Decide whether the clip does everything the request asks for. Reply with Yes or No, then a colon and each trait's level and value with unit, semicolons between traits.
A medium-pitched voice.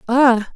No: high, 245 Hz